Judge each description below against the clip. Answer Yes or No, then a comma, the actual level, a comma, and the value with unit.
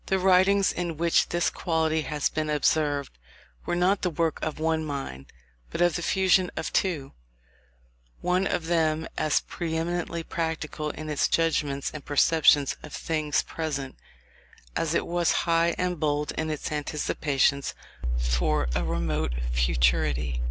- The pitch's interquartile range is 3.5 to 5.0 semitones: No, average, 3.1 semitones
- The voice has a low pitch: No, medium, 155 Hz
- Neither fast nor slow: Yes, average, 145 wpm